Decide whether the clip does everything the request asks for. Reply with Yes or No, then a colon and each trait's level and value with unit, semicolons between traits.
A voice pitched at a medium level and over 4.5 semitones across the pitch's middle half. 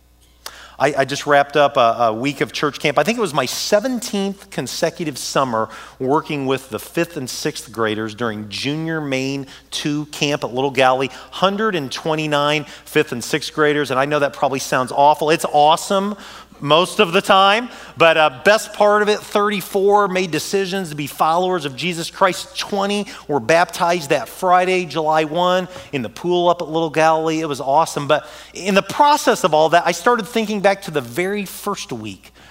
Yes: medium, 160 Hz; wide, 5.4 semitones